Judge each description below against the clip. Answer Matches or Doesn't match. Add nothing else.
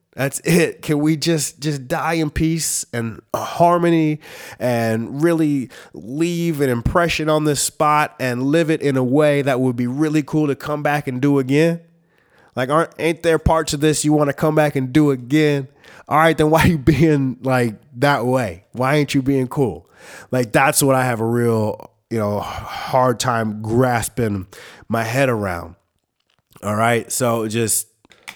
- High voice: Doesn't match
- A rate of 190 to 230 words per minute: Doesn't match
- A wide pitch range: Doesn't match